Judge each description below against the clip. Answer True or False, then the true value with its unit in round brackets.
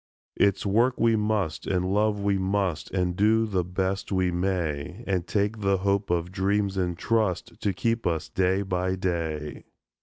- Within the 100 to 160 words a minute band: False (170 wpm)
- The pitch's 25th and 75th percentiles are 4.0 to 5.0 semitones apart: False (2.4 semitones)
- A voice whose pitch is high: False (95 Hz)